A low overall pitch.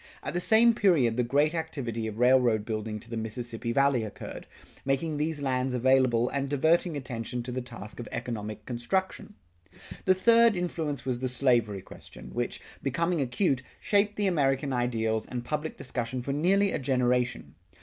Yes: low, 130 Hz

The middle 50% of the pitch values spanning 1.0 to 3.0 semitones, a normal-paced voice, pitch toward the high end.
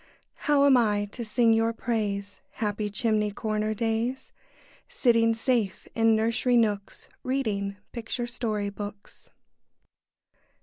No: narrow, 2.4 semitones; slow, 115 wpm; high, 225 Hz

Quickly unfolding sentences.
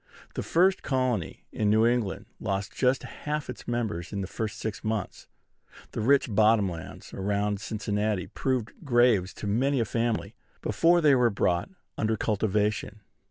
No: average, 155 wpm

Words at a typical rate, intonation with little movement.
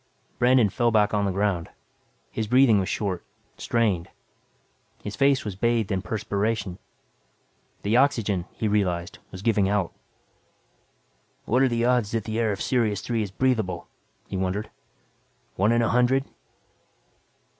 No: average, 145 wpm; average, 3.2 semitones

